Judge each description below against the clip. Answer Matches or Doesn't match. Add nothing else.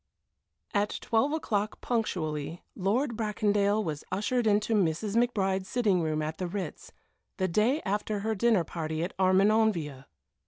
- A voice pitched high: Matches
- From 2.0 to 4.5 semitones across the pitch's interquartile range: Matches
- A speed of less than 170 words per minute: Matches